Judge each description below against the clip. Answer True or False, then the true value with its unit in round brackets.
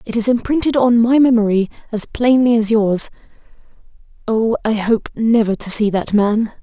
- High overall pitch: True (225 Hz)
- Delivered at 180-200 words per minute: False (165 wpm)